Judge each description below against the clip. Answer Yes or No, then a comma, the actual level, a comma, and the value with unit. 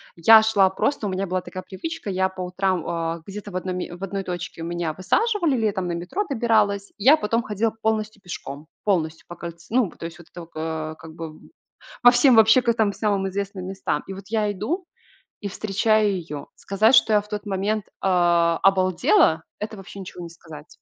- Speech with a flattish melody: No, average, 3.7 semitones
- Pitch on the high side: Yes, high, 195 Hz